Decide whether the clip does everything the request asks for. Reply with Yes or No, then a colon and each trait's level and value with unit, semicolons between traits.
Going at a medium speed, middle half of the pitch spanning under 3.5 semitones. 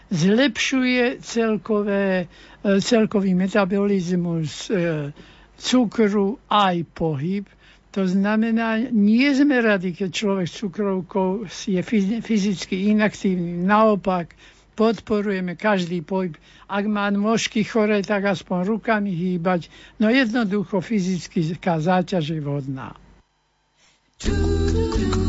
No: slow, 90 wpm; average, 3.1 semitones